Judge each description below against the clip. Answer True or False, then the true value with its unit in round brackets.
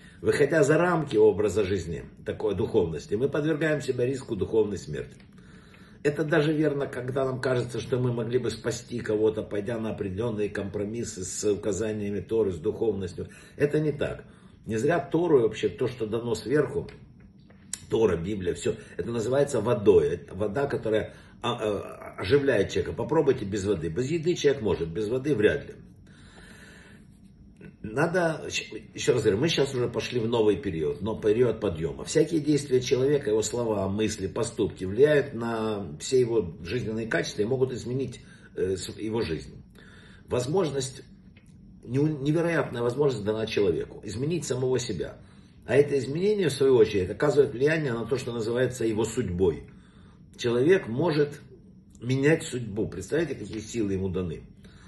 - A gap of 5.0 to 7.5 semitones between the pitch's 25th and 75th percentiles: True (5.6 semitones)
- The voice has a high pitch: False (125 Hz)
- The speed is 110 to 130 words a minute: False (140 wpm)